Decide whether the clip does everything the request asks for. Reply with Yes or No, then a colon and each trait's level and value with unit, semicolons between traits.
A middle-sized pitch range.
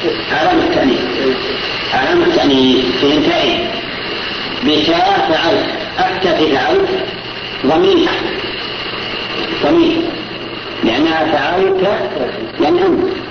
No: narrow, 1.8 semitones